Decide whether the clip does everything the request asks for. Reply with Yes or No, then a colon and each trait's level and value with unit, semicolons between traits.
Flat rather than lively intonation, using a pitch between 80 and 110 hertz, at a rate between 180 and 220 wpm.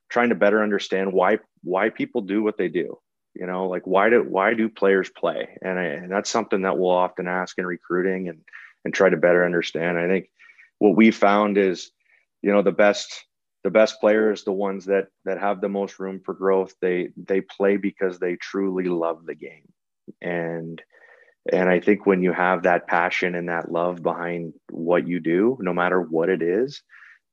Yes: narrow, 2.2 semitones; very low, 95 Hz; average, 200 wpm